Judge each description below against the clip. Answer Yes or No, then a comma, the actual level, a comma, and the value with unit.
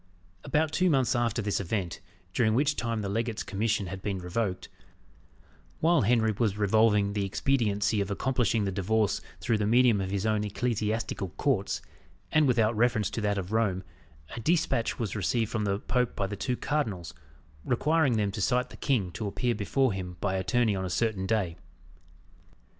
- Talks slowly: No, average, 175 wpm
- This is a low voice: Yes, low, 110 Hz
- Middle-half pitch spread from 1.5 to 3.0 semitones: No, average, 3.4 semitones